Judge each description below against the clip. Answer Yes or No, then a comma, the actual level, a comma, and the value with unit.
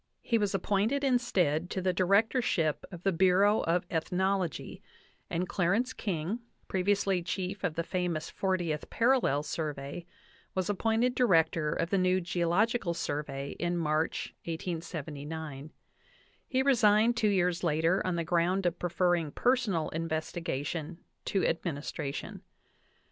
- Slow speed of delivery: Yes, slow, 130 wpm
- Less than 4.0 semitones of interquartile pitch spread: Yes, average, 3.6 semitones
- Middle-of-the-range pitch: Yes, medium, 180 Hz